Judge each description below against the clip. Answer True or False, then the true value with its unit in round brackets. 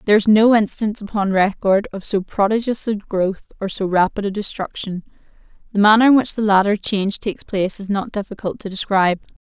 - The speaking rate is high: False (190 wpm)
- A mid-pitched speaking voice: False (205 Hz)